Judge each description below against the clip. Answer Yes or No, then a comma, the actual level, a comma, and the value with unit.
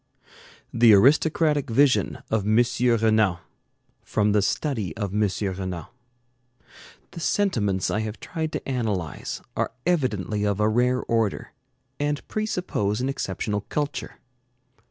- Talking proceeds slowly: Yes, slow, 120 wpm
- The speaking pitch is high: No, low, 110 Hz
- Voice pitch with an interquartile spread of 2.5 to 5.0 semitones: No, wide, 5.5 semitones